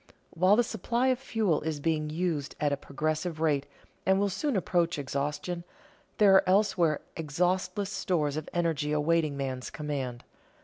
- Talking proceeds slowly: No, average, 160 wpm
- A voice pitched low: No, medium, 165 Hz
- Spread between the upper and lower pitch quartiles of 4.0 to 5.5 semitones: Yes, average, 4.4 semitones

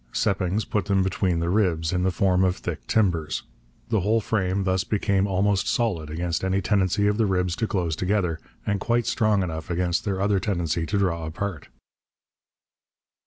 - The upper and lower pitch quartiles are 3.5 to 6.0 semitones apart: No, average, 2.7 semitones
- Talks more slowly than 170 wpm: No, average, 175 wpm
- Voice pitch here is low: Yes, very low, 95 Hz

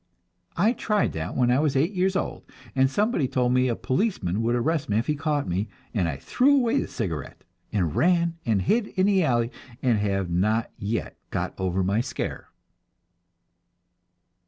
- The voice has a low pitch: Yes, low, 125 Hz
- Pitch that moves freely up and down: Yes, wide, 9.0 semitones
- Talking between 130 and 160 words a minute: No, average, 180 wpm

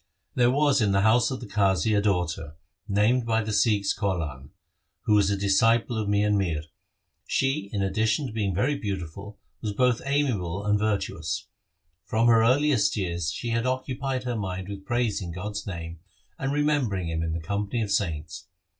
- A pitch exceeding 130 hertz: No, low, 105 Hz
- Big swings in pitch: No, average, 3.8 semitones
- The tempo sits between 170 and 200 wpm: Yes, average, 180 wpm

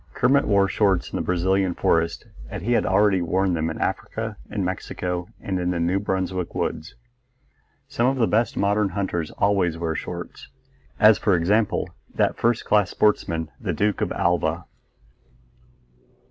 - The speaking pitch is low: Yes, very low, 95 Hz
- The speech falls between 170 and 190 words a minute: No, average, 160 wpm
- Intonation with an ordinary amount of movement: Yes, average, 3.2 semitones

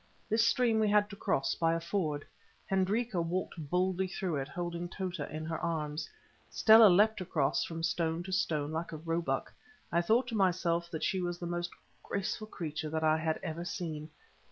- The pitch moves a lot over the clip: No, average, 3.0 semitones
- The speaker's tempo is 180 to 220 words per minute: Yes, average, 185 wpm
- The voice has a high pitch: No, medium, 170 Hz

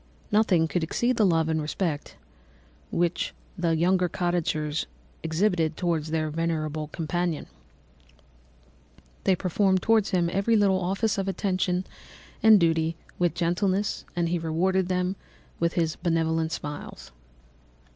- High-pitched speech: No, medium, 175 Hz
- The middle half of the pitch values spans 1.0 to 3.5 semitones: Yes, average, 2.7 semitones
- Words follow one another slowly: Yes, slow, 125 wpm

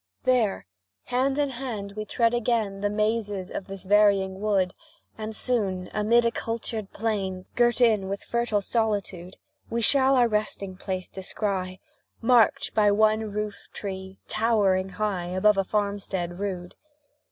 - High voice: Yes, high, 210 Hz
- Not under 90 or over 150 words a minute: Yes, average, 140 wpm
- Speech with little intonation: No, average, 3.0 semitones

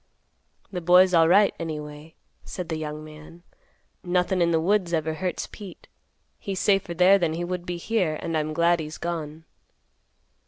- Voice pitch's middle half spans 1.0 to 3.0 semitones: Yes, narrow, 2.5 semitones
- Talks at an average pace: Yes, average, 160 wpm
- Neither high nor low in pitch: Yes, medium, 170 Hz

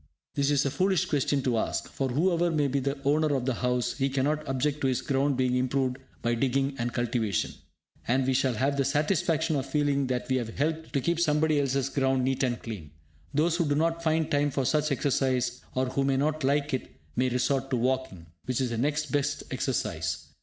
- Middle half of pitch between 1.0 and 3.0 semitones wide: Yes, narrow, 2.6 semitones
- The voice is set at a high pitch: No, low, 135 Hz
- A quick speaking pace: Yes, fast, 215 wpm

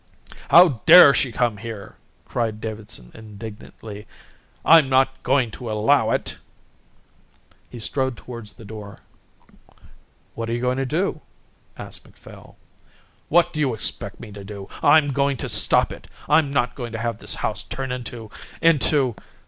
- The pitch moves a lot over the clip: No, average, 4.1 semitones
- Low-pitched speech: Yes, low, 120 Hz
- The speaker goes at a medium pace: Yes, average, 150 wpm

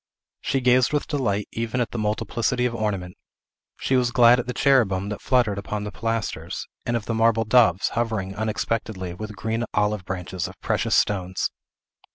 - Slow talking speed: No, average, 175 wpm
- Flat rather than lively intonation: No, average, 3.0 semitones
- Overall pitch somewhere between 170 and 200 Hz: No, low, 110 Hz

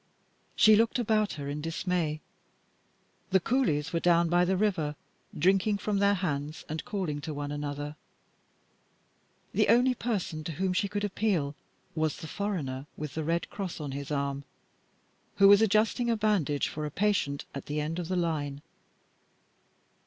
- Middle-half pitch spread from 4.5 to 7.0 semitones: Yes, wide, 5.5 semitones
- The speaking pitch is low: No, medium, 170 Hz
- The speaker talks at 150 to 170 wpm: Yes, average, 160 wpm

